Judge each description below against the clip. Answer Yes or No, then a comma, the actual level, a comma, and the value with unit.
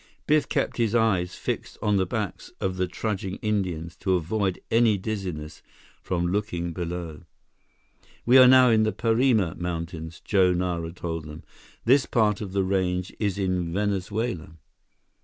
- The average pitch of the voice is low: Yes, very low, 95 Hz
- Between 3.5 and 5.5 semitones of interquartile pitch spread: Yes, average, 3.8 semitones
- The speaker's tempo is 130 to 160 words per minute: Yes, average, 150 wpm